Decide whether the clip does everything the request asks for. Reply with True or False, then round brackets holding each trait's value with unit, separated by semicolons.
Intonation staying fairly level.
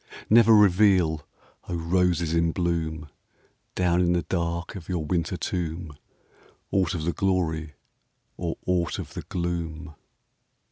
True (1.8 semitones)